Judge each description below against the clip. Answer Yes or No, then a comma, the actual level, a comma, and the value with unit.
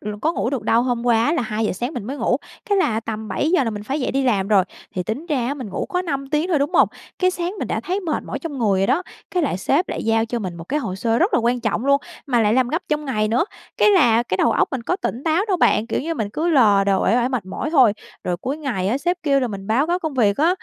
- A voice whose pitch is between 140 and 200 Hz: No, very high, 250 Hz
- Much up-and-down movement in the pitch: Yes, wide, 5.8 semitones